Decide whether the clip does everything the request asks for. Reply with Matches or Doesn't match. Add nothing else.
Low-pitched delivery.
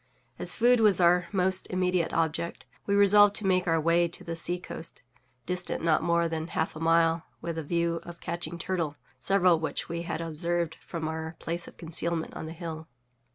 Doesn't match